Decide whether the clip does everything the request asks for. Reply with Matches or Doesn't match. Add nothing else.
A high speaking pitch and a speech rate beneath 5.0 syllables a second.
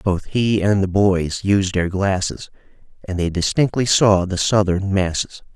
Doesn't match